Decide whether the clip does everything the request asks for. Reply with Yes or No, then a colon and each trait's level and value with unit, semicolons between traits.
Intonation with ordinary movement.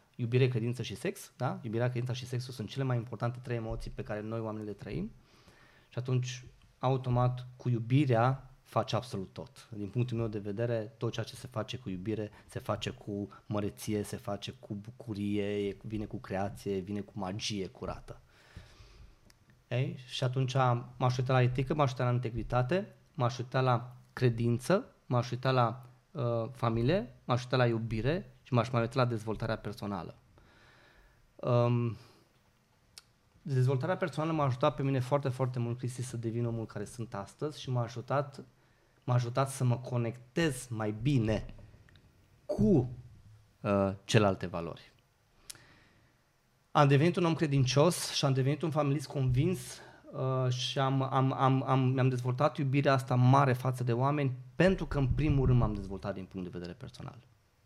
Yes: average, 3.1 semitones